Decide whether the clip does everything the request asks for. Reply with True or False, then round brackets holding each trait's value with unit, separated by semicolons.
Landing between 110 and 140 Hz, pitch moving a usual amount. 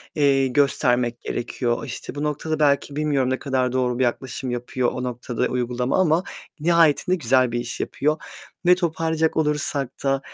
True (135 Hz; 3.4 semitones)